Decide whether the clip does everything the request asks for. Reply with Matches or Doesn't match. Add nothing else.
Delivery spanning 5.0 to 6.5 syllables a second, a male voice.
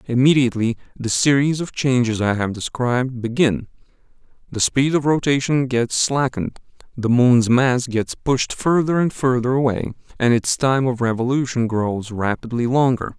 Doesn't match